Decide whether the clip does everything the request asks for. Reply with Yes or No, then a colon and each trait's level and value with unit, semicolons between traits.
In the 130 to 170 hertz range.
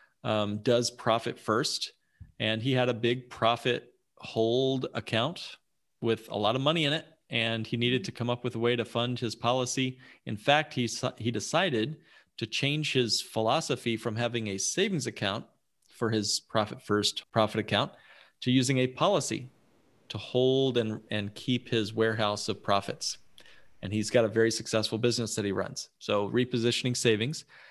No: low, 120 Hz